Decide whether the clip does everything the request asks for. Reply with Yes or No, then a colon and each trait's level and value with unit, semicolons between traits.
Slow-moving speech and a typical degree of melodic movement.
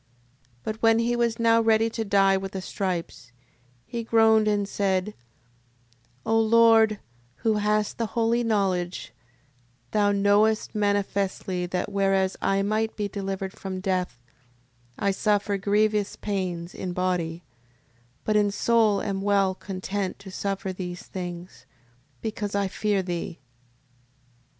No: slow, 130 wpm; narrow, 2.3 semitones